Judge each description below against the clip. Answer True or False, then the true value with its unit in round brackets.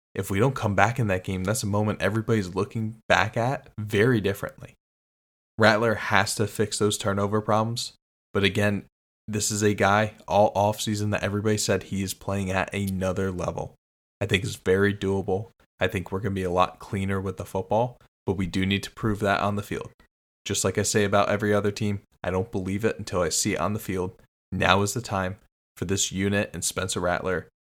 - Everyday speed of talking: False (210 wpm)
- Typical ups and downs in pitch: False (1.9 semitones)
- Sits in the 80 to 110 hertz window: True (100 Hz)